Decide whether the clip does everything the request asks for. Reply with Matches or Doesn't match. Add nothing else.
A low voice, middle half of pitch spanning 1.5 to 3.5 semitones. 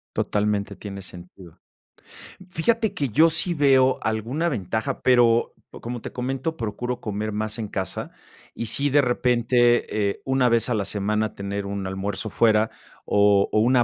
Doesn't match